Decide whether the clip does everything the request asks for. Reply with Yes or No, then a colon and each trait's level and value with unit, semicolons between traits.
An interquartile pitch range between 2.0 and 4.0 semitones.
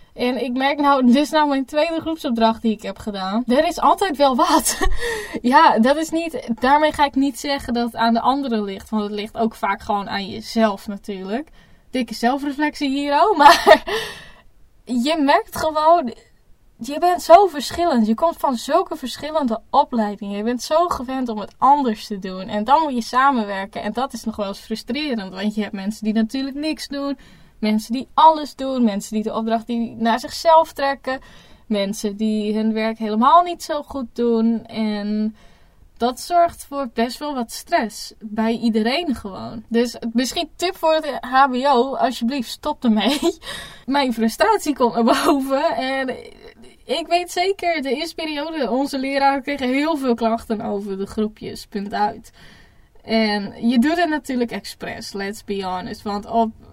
No: average, 4.7 semitones